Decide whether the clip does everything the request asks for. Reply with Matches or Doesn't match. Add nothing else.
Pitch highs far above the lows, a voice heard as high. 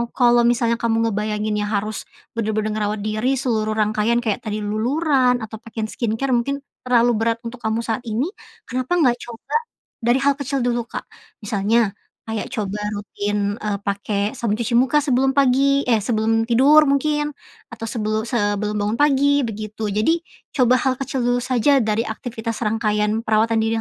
Doesn't match